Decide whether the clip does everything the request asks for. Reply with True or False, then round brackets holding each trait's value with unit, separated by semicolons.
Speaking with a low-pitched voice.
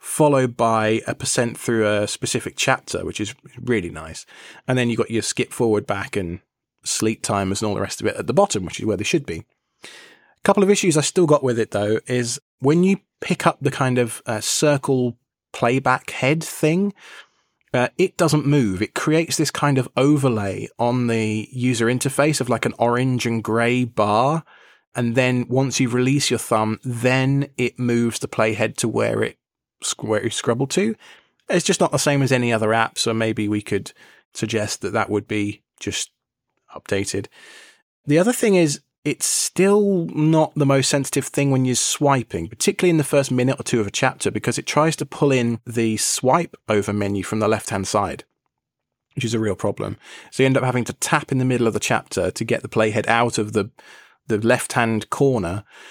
True (125 Hz)